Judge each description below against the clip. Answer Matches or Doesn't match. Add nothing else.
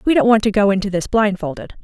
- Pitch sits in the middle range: Doesn't match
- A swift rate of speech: Matches